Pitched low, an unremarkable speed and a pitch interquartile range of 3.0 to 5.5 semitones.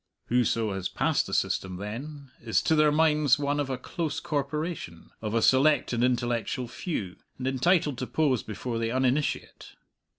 Yes: low, 130 Hz; average, 165 wpm; average, 4.5 semitones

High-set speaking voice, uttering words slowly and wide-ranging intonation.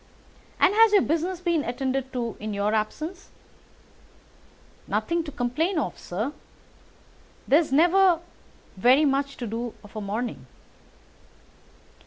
Yes: very high, 275 Hz; slow, 120 wpm; wide, 6.4 semitones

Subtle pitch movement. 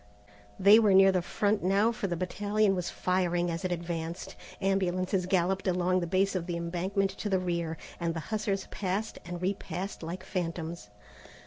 Yes: narrow, 2.2 semitones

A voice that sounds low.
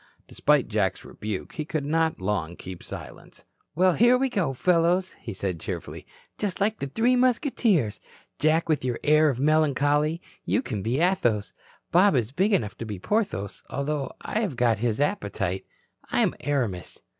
No: medium, 150 Hz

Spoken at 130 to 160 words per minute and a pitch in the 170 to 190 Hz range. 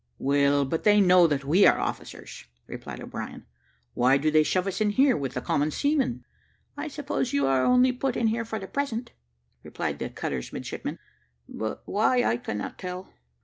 No: average, 185 wpm; medium, 185 Hz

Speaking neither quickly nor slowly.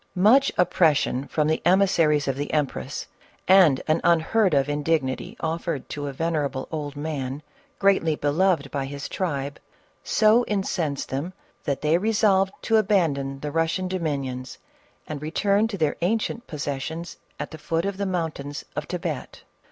Yes: average, 160 wpm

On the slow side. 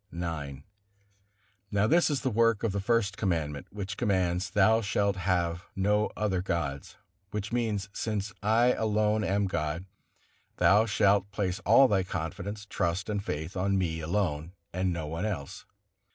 No: average, 155 wpm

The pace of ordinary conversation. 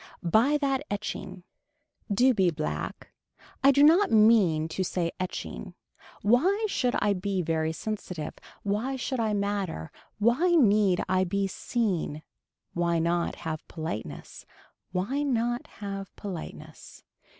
No: slow, 125 wpm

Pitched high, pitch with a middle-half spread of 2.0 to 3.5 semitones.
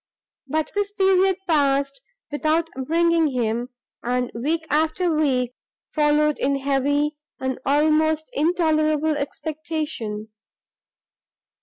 Yes: very high, 300 Hz; narrow, 2.5 semitones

